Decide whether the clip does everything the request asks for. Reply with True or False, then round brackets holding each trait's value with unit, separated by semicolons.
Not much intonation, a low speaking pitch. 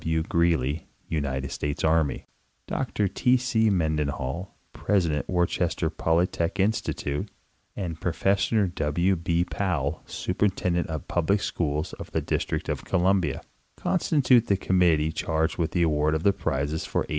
False (3.7 semitones; 85 Hz)